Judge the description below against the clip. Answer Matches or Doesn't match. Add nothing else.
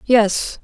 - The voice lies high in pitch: Matches